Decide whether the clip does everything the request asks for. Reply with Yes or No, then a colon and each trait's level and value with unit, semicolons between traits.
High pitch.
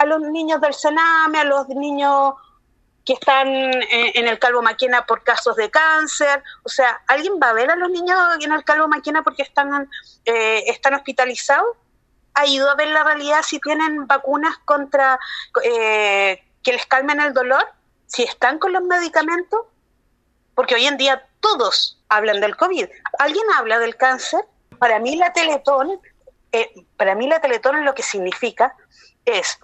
Yes: very high, 285 Hz